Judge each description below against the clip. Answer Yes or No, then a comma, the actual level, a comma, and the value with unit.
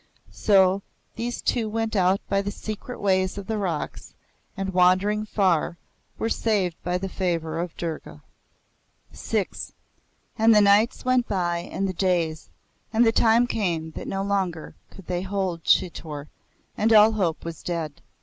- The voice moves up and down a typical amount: Yes, average, 3.5 semitones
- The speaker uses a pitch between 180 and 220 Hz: Yes, high, 190 Hz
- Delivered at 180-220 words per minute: No, average, 155 wpm